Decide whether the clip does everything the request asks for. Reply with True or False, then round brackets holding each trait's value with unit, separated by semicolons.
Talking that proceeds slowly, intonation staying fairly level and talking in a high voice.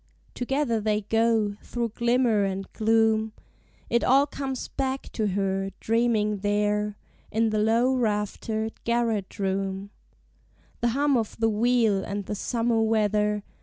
True (130 wpm; 2.2 semitones; 220 Hz)